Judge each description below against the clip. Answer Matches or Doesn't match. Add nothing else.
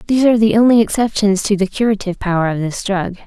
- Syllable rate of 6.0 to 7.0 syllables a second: Matches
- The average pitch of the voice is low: Doesn't match